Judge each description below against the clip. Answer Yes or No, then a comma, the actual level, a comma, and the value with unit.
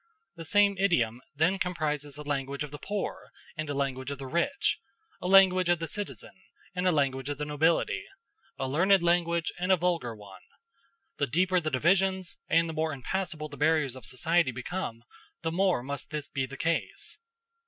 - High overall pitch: No, medium, 160 Hz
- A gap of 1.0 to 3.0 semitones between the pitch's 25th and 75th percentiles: No, average, 4.4 semitones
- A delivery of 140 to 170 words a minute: No, average, 185 wpm